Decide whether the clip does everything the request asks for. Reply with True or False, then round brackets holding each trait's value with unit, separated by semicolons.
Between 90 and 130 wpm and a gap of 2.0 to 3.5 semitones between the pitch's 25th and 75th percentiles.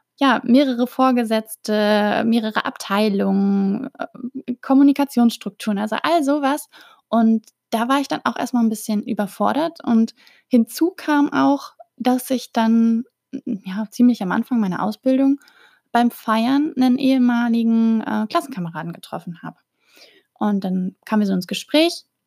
False (125 wpm; 4.0 semitones)